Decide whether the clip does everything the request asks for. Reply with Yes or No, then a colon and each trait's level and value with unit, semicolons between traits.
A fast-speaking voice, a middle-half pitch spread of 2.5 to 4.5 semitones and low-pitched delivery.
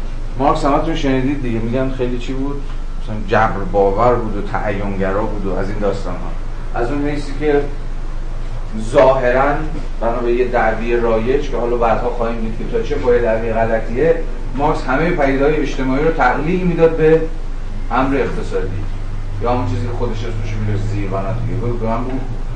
Yes: fast, 165 wpm; average, 3.7 semitones; low, 120 Hz